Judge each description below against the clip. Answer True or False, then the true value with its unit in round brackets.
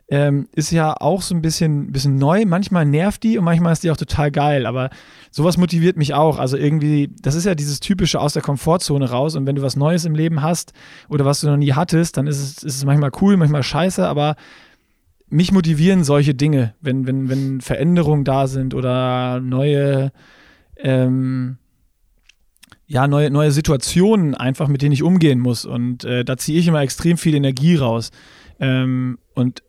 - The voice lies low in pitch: False (145 Hz)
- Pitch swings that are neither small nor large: True (3.4 semitones)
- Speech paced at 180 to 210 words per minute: True (190 wpm)